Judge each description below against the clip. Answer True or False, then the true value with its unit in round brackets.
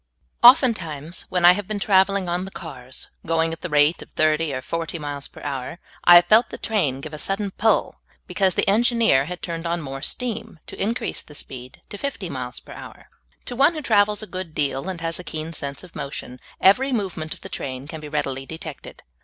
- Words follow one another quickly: True (220 wpm)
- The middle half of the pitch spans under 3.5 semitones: False (5.3 semitones)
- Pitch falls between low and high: True (170 Hz)